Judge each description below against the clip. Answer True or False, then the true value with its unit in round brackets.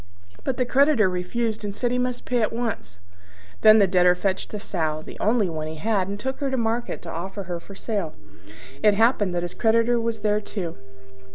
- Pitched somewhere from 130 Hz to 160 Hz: False (210 Hz)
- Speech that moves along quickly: True (210 wpm)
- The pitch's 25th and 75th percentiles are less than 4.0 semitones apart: False (4.7 semitones)